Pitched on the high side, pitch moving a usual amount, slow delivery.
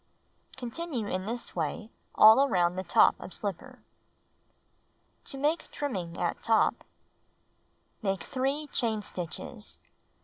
No: high, 220 Hz; wide, 6.3 semitones; slow, 105 wpm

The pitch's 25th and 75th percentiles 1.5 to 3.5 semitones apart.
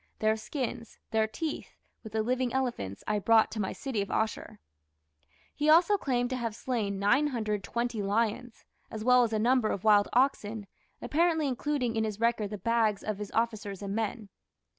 Yes: average, 3.0 semitones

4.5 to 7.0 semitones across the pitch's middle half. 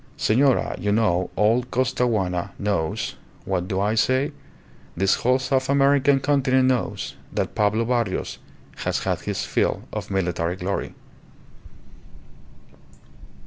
Yes: average, 5.1 semitones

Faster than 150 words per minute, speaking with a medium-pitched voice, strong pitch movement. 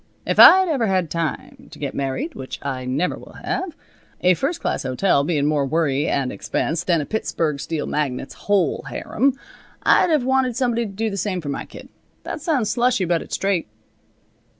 Yes: average, 190 wpm; medium, 180 Hz; wide, 8.9 semitones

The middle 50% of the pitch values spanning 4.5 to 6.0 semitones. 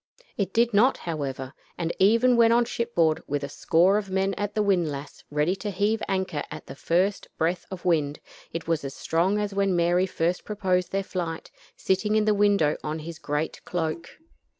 No: average, 4.1 semitones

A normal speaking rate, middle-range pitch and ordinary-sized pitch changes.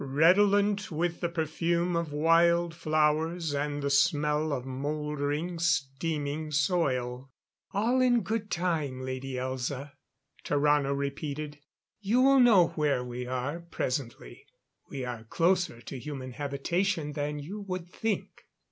No: slow, 125 wpm; medium, 150 Hz; average, 3.7 semitones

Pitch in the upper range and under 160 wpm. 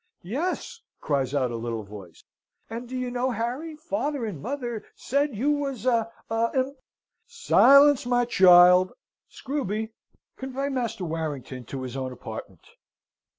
Yes: high, 230 Hz; average, 145 wpm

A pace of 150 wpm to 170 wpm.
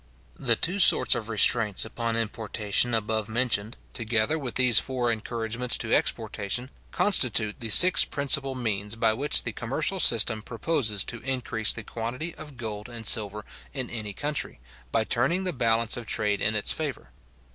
Yes: average, 160 wpm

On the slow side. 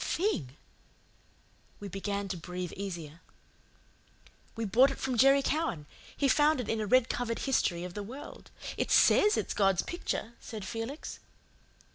No: average, 150 wpm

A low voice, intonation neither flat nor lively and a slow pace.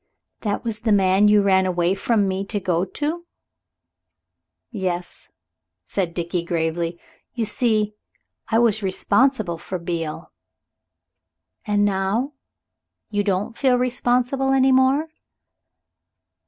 No: high, 205 Hz; average, 4.7 semitones; slow, 115 wpm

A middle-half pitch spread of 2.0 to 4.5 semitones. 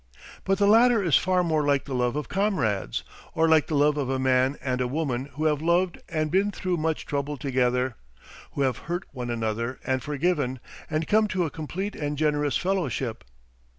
No: average, 5.1 semitones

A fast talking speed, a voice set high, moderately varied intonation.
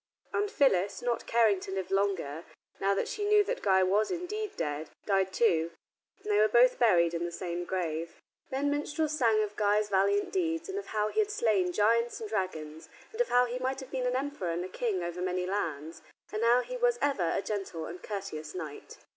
No: fast, 215 wpm; high, 205 Hz; wide, 6.2 semitones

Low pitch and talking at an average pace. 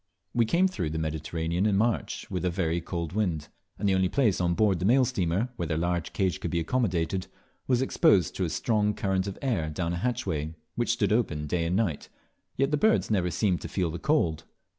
No: very low, 95 Hz; fast, 220 wpm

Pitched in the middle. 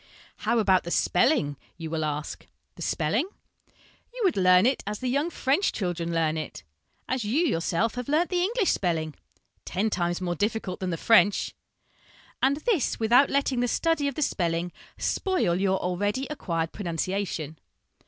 No: high, 205 Hz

